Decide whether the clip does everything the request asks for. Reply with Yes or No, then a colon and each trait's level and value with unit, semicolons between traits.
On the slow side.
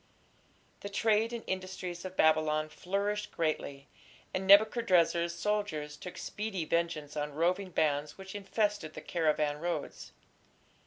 Yes: slow, 120 wpm